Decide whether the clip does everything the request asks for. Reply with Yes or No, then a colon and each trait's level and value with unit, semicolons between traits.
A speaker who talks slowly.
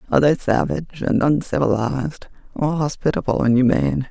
Yes: slow, 130 wpm